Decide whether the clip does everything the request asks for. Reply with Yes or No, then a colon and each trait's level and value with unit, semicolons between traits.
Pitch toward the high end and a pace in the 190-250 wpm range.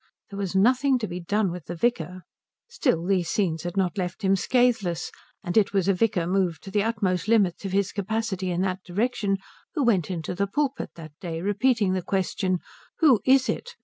Yes: high, 195 Hz; average, 200 wpm